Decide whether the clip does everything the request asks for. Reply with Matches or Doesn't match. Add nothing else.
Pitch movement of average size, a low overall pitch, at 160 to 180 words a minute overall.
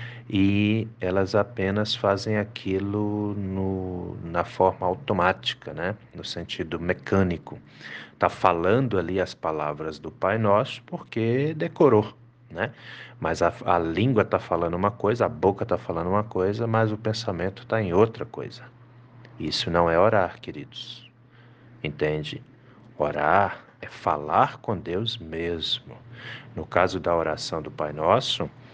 Doesn't match